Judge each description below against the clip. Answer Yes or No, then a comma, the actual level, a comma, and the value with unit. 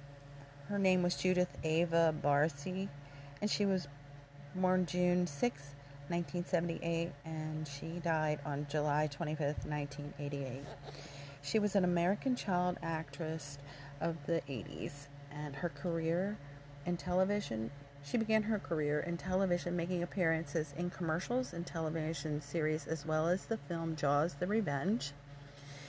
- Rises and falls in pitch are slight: No, average, 3.8 semitones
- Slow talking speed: Yes, slow, 130 wpm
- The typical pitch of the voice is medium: Yes, medium, 160 Hz